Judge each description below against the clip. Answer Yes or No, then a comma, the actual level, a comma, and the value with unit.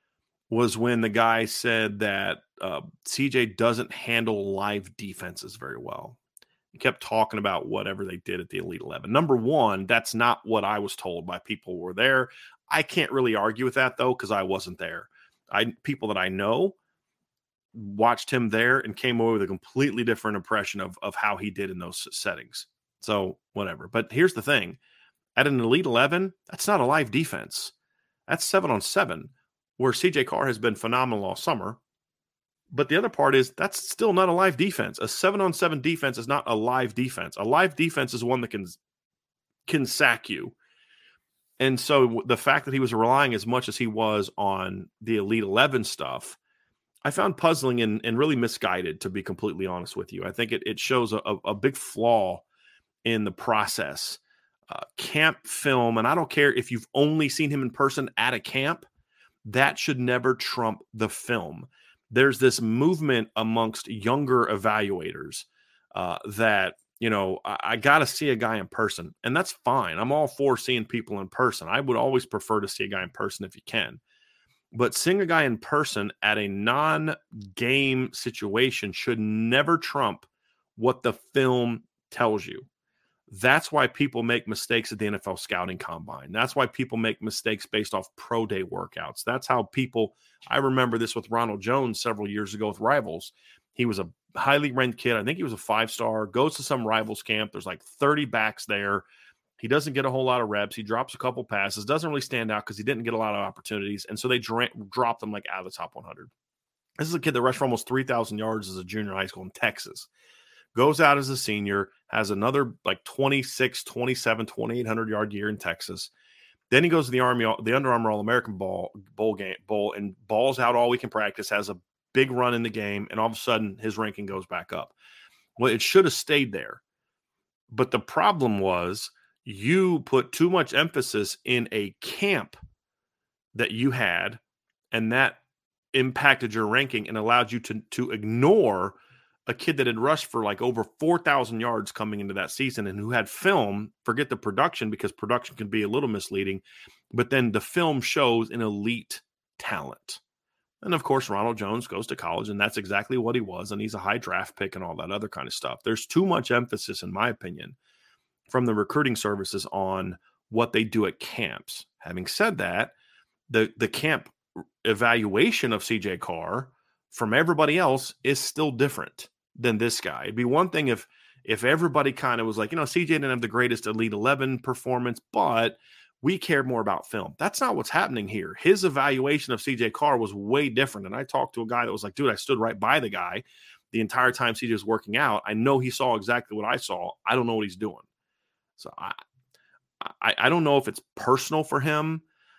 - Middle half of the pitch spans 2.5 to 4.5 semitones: Yes, average, 3.9 semitones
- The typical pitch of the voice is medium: No, low, 115 Hz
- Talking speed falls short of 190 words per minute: No, average, 200 wpm